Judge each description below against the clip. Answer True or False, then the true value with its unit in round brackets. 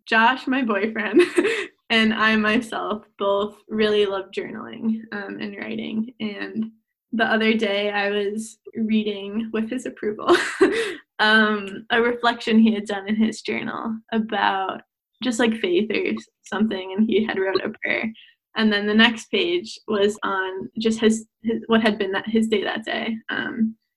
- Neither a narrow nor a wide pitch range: False (1.5 semitones)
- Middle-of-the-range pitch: False (220 Hz)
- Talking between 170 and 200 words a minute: False (160 wpm)